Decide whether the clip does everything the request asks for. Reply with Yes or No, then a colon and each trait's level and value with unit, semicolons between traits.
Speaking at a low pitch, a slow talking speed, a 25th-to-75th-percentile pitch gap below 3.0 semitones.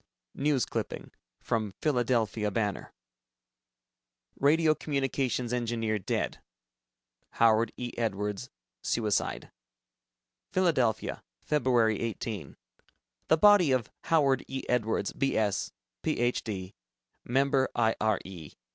No: low, 120 Hz; slow, 90 wpm; average, 3.8 semitones